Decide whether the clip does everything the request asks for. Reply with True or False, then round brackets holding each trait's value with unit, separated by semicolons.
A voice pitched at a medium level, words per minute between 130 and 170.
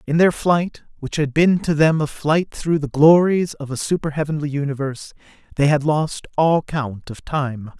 False (150 Hz; 190 wpm)